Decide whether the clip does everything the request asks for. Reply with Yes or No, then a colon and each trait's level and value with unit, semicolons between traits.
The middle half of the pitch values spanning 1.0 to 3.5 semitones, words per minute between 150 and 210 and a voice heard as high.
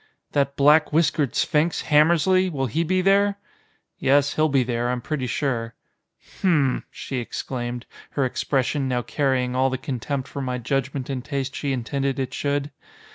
No: average, 2.9 semitones; average, 165 wpm; medium, 140 Hz